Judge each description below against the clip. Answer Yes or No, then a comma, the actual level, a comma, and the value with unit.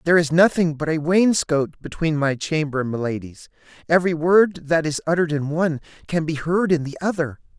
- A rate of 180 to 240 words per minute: Yes, average, 190 wpm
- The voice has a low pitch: No, medium, 160 Hz